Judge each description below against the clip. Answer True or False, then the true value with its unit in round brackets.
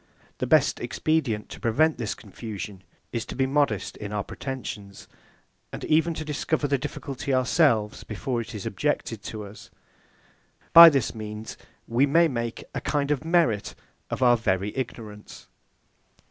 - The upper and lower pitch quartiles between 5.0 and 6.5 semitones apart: True (5.5 semitones)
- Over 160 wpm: False (150 wpm)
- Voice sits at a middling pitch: False (120 Hz)